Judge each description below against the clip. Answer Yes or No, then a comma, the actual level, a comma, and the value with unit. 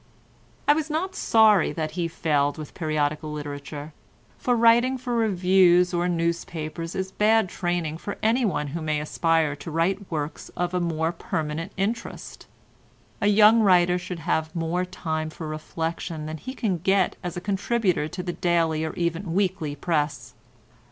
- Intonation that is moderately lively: Yes, average, 3.6 semitones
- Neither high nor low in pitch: Yes, medium, 175 Hz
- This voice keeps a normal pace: Yes, average, 155 wpm